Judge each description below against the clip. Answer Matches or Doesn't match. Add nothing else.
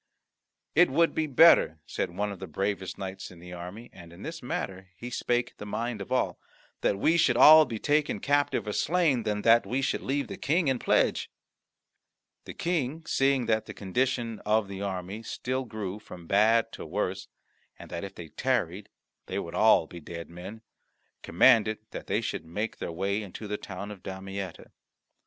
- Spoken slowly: Doesn't match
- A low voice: Matches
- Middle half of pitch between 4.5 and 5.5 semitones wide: Matches